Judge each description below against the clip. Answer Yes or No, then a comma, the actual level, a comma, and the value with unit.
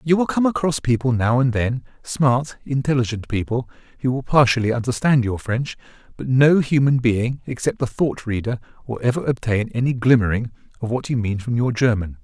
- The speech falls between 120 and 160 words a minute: No, average, 170 wpm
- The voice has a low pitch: Yes, low, 125 Hz